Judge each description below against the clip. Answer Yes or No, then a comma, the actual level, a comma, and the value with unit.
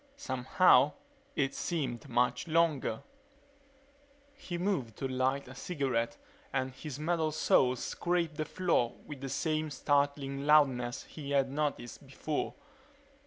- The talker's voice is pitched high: No, medium, 140 Hz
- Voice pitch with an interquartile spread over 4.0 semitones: No, average, 3.1 semitones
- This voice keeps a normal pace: No, slow, 120 wpm